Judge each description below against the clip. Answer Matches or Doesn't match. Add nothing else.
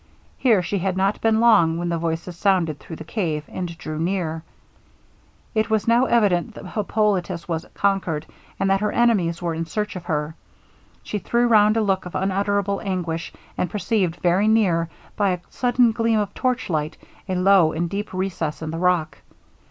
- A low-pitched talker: Doesn't match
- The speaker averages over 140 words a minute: Matches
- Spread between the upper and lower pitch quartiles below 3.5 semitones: Doesn't match